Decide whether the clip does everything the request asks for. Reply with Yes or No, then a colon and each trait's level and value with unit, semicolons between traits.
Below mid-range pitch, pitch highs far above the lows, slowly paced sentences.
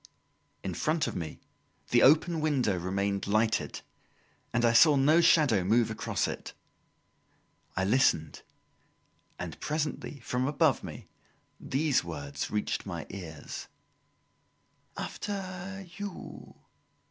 Yes: low, 125 Hz; wide, 8.0 semitones; slow, 110 wpm